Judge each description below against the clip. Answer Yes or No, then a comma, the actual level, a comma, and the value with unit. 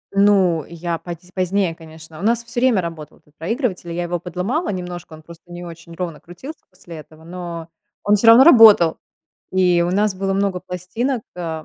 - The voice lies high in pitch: No, medium, 180 Hz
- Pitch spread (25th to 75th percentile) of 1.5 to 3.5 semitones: Yes, average, 3.2 semitones